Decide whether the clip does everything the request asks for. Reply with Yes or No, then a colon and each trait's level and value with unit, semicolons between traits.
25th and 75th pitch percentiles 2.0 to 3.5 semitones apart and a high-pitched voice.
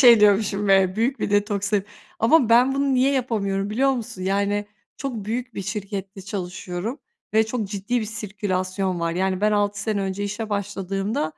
Yes: narrow, 2.6 semitones; high, 205 Hz